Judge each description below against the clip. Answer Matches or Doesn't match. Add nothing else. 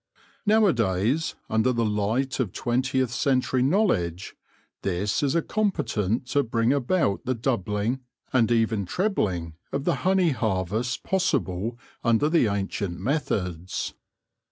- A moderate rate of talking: Doesn't match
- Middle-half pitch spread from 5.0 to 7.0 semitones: Matches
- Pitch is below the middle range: Matches